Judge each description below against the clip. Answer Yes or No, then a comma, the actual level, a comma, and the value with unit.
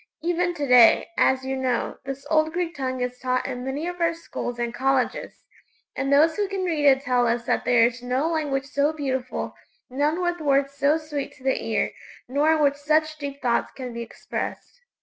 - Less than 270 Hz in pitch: No, very high, 280 Hz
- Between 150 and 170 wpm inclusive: No, fast, 205 wpm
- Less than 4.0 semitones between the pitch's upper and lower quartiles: Yes, average, 3.4 semitones